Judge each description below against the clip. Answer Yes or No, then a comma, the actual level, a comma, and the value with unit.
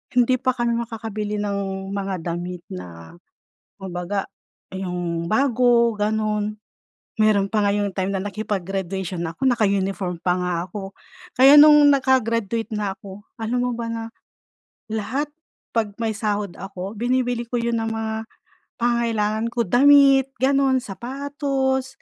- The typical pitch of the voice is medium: No, high, 215 Hz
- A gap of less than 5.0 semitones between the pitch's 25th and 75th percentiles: Yes, average, 3.8 semitones